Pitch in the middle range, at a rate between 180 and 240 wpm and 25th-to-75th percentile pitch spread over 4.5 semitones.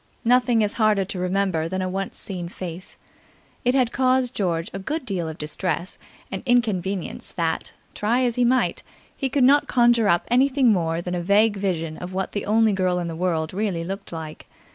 No: high, 195 Hz; average, 195 wpm; average, 5.2 semitones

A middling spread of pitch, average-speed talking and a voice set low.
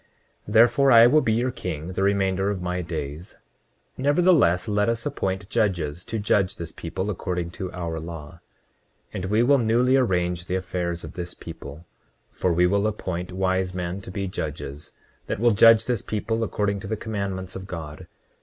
Yes: average, 4.0 semitones; average, 180 wpm; very low, 95 Hz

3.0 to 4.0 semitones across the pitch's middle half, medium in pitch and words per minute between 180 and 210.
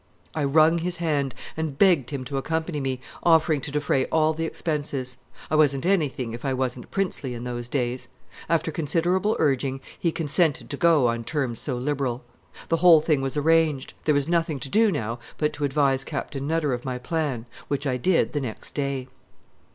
Yes: average, 3.6 semitones; medium, 145 Hz; average, 190 wpm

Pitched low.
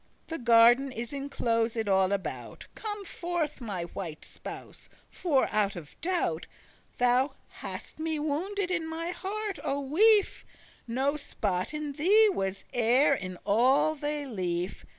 No: very high, 275 Hz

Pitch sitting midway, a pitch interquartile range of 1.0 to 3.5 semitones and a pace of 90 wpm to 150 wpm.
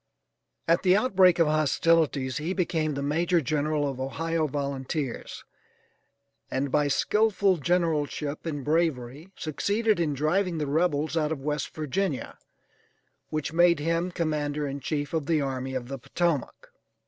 Yes: medium, 155 Hz; average, 3.1 semitones; average, 140 wpm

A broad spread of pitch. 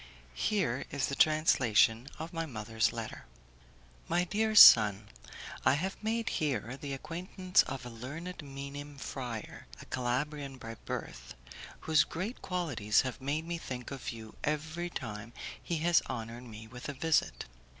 Yes: wide, 5.8 semitones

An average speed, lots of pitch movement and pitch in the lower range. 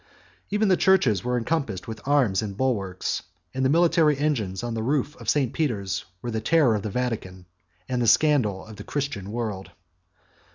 Yes: average, 180 wpm; wide, 5.9 semitones; low, 120 Hz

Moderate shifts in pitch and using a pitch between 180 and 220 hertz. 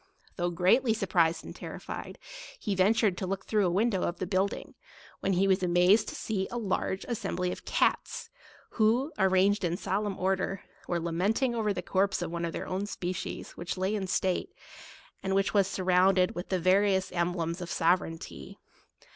No: narrow, 2.2 semitones; high, 190 Hz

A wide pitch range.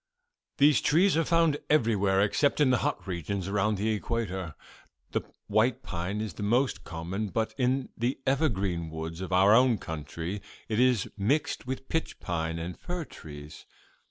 Yes: wide, 6.2 semitones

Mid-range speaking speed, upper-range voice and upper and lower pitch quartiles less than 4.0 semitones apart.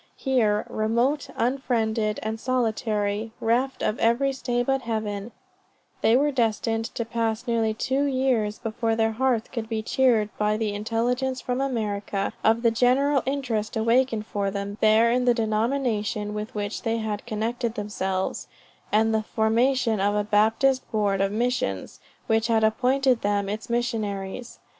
Yes: average, 150 wpm; high, 225 Hz; average, 2.7 semitones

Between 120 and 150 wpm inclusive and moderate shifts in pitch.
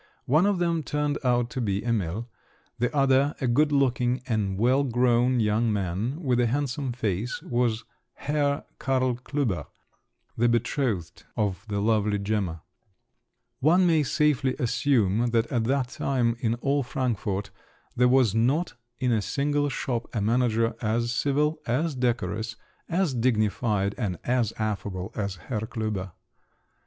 Yes: average, 145 wpm; average, 3.9 semitones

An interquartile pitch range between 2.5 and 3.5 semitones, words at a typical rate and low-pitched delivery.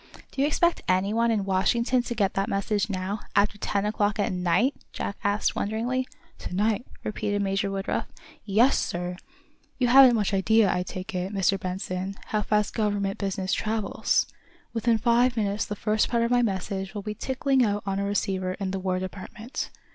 No: average, 2.8 semitones; average, 180 wpm; high, 205 Hz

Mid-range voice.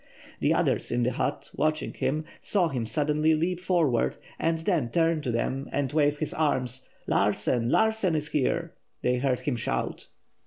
Yes: medium, 150 Hz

